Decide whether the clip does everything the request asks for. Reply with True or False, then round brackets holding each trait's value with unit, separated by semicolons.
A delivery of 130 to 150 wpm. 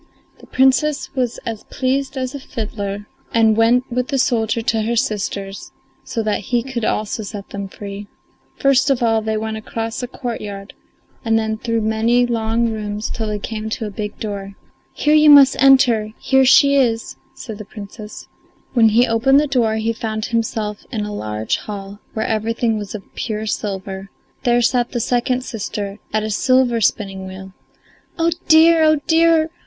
False (175 wpm)